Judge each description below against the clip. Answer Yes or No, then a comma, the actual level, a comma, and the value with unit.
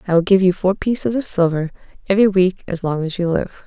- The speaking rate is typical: No, fast, 245 wpm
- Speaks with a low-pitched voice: No, medium, 185 Hz